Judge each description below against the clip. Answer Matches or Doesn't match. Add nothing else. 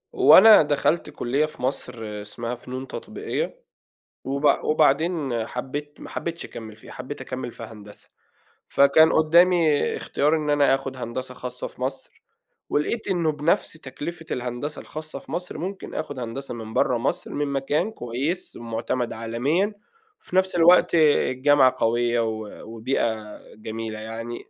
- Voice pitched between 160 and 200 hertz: Doesn't match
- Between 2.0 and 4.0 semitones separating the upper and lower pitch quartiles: Doesn't match